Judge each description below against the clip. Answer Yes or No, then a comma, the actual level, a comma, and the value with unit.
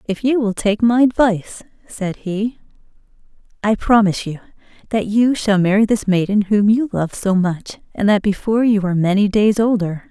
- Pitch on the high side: Yes, high, 205 Hz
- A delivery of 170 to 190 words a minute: Yes, average, 180 wpm